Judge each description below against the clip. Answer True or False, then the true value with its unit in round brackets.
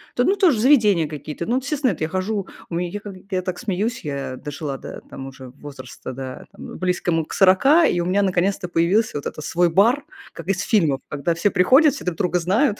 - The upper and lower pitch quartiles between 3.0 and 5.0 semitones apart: False (5.4 semitones)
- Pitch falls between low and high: True (180 Hz)